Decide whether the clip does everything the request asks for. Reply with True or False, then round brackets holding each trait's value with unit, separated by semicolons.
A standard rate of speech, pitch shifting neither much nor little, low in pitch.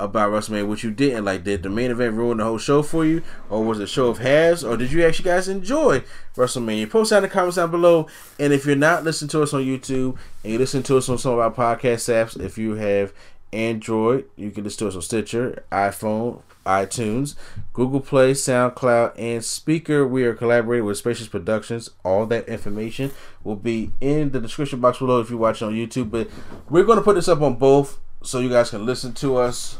False (225 wpm; 4.0 semitones; 120 Hz)